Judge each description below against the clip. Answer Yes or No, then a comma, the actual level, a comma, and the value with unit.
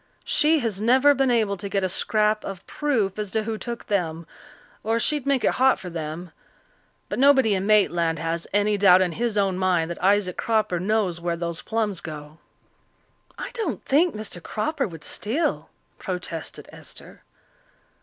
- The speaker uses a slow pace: No, average, 170 wpm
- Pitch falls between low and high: No, high, 205 Hz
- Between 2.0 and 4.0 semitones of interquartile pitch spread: No, average, 4.7 semitones